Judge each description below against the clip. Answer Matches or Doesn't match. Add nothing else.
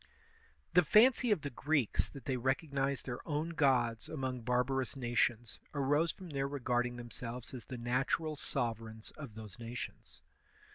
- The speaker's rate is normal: Matches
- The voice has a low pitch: Matches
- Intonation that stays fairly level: Doesn't match